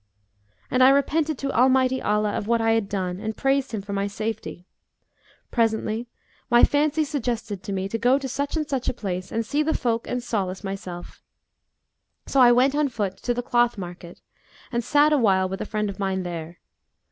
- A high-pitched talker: Yes, high, 230 Hz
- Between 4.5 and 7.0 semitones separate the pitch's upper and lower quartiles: Yes, average, 4.9 semitones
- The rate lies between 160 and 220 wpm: Yes, average, 195 wpm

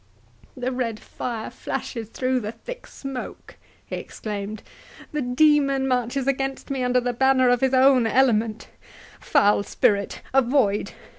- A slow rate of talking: Yes, slow, 130 wpm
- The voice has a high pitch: Yes, very high, 250 Hz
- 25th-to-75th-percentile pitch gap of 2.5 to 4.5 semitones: Yes, average, 2.9 semitones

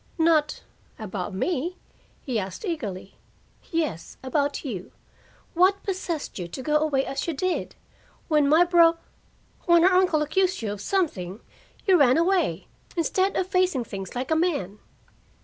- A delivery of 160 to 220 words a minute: No, average, 150 wpm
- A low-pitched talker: No, very high, 310 Hz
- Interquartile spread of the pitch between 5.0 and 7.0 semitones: Yes, wide, 6.6 semitones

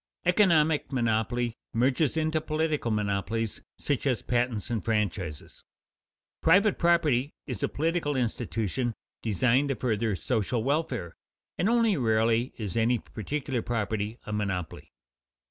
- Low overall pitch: Yes, low, 120 Hz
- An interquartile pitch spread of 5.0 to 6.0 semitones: Yes, wide, 5.4 semitones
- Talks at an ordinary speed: No, slow, 120 wpm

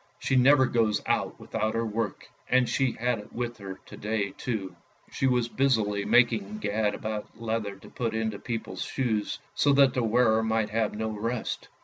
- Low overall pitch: Yes, low, 110 Hz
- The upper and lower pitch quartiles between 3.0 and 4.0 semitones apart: No, narrow, 2.5 semitones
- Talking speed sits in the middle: Yes, average, 180 wpm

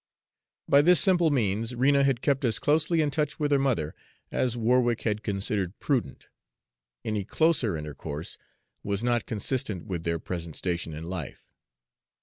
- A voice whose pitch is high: No, low, 115 Hz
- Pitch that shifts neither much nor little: No, wide, 6.9 semitones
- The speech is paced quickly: No, average, 150 wpm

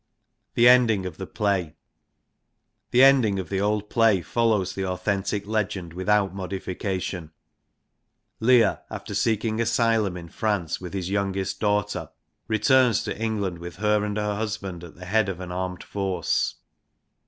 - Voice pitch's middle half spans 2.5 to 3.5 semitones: Yes, average, 2.9 semitones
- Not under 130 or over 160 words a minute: Yes, average, 145 wpm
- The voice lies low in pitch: Yes, low, 100 Hz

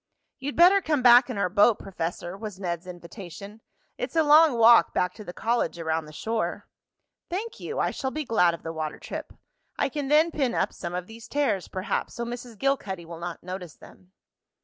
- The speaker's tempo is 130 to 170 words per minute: No, average, 200 wpm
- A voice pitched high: Yes, high, 215 Hz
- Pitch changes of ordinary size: No, wide, 7.0 semitones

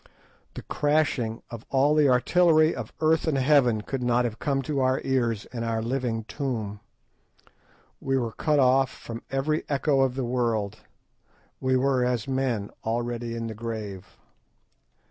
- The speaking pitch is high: No, low, 125 Hz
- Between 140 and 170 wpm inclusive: Yes, average, 150 wpm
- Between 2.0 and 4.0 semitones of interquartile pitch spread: Yes, average, 2.9 semitones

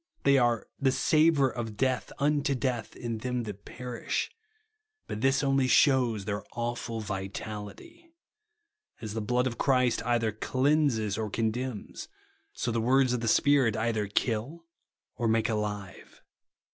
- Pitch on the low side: Yes, low, 120 Hz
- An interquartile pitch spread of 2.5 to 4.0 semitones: Yes, average, 3.5 semitones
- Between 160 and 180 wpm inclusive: No, average, 145 wpm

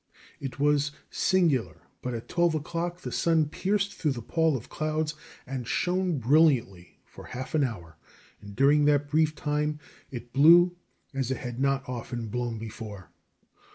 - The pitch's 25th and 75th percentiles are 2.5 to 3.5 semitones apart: No, average, 4.5 semitones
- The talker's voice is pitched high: No, medium, 140 Hz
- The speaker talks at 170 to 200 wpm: No, average, 155 wpm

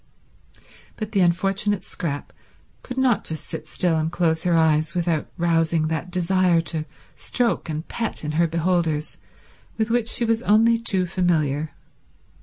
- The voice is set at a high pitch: No, medium, 175 Hz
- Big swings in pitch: No, average, 3.9 semitones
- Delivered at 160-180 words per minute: No, average, 150 wpm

